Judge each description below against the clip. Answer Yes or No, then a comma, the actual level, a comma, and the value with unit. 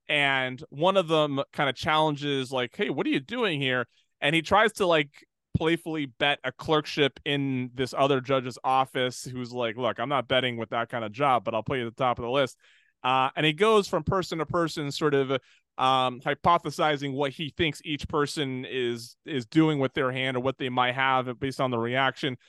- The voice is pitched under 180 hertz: Yes, medium, 140 Hz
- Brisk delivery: Yes, fast, 215 wpm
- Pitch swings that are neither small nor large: Yes, average, 3.2 semitones